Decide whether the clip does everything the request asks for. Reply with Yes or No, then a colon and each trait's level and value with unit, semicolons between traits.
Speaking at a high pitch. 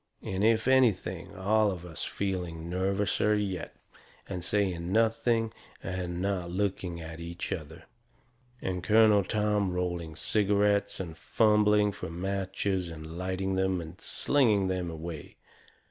No: very low, 95 Hz